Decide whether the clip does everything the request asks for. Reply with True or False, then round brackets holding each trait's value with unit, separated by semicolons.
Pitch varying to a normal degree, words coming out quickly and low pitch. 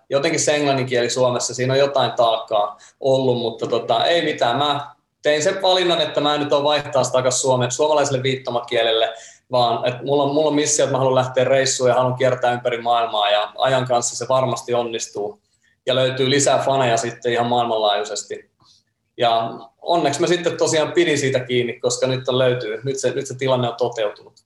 True (3.1 semitones; 180 wpm; 130 Hz)